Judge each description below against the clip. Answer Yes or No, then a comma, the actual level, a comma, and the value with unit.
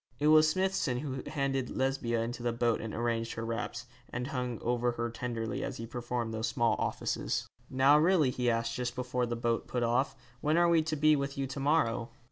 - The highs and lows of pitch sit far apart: No, average, 3.0 semitones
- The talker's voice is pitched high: No, low, 125 Hz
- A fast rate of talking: Yes, fast, 210 wpm